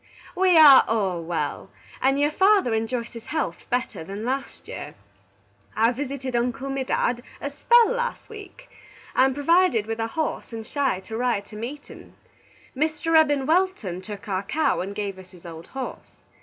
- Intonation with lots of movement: Yes, wide, 6.1 semitones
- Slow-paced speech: No, average, 170 wpm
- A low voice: No, very high, 255 Hz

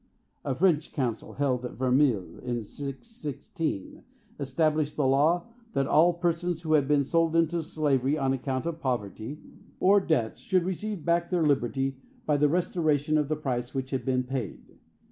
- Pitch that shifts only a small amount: No, average, 4.0 semitones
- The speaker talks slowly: No, average, 165 wpm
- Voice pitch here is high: No, medium, 145 Hz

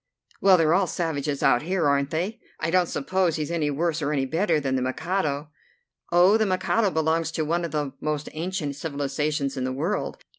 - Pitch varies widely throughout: No, average, 3.5 semitones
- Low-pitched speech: No, medium, 160 Hz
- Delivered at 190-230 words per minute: Yes, average, 195 wpm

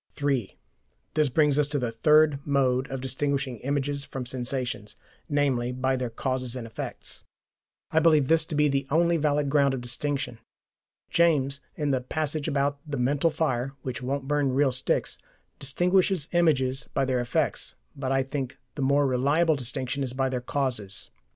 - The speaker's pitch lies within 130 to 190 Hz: Yes, medium, 140 Hz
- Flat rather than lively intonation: Yes, narrow, 2.3 semitones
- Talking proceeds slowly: No, average, 165 wpm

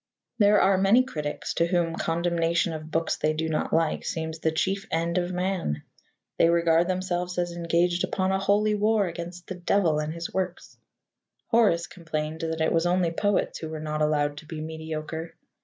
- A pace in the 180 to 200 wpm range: Yes, average, 185 wpm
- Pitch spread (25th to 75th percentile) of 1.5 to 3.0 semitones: Yes, narrow, 2.4 semitones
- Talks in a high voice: No, medium, 170 Hz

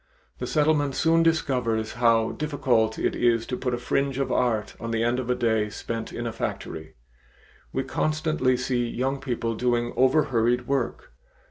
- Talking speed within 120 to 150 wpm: No, average, 165 wpm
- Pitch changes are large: No, average, 3.0 semitones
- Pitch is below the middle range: Yes, low, 125 Hz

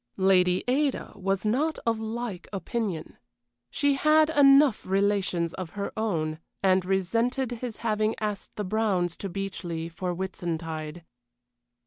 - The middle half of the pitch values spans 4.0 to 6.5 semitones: Yes, average, 4.3 semitones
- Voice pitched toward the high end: Yes, high, 200 Hz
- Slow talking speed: Yes, slow, 125 wpm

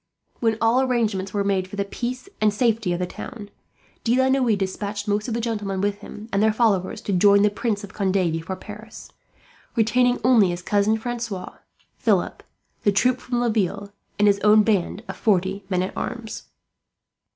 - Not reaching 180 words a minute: No, average, 185 wpm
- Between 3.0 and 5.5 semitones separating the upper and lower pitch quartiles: No, narrow, 2.6 semitones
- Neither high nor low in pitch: No, high, 210 Hz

